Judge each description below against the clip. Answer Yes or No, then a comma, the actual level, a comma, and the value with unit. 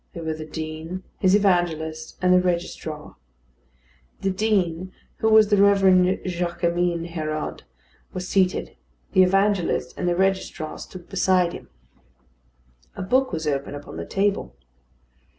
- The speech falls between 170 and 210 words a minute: No, slow, 135 wpm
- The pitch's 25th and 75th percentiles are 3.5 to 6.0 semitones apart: No, average, 3.0 semitones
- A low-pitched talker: No, medium, 180 Hz